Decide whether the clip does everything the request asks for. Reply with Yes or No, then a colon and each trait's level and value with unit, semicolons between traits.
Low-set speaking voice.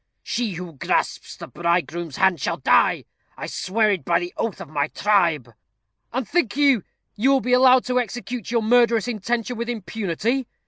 No: high, 220 Hz